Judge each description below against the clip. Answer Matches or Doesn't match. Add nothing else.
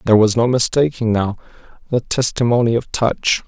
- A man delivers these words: Matches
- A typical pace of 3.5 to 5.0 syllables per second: Doesn't match